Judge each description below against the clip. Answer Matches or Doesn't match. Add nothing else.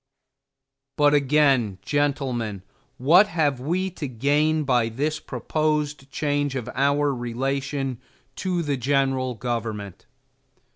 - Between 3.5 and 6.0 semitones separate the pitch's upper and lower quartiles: Doesn't match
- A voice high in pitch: Doesn't match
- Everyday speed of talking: Doesn't match